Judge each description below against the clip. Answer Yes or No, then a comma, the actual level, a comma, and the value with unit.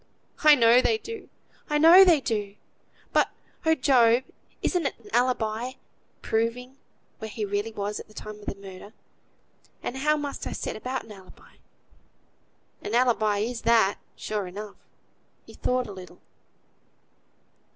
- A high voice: Yes, high, 230 Hz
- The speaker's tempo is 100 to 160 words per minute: Yes, average, 150 wpm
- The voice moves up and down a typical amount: Yes, average, 4.0 semitones